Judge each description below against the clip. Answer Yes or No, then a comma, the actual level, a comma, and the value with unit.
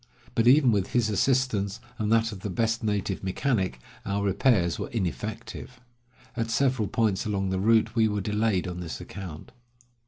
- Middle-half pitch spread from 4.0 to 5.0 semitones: No, average, 3.0 semitones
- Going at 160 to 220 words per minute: Yes, average, 165 wpm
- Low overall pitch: Yes, low, 105 Hz